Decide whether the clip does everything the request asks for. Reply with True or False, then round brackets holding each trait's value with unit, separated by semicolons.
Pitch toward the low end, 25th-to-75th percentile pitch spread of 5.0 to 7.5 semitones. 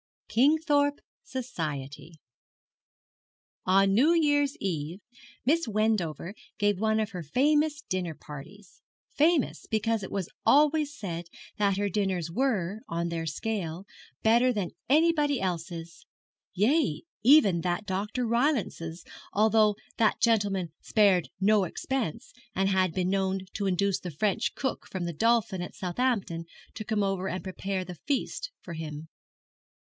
False (200 Hz; 5.5 semitones)